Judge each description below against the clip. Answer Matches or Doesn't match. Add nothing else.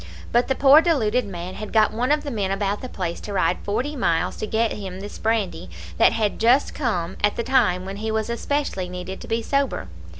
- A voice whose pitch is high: Matches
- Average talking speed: Doesn't match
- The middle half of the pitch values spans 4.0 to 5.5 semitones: Matches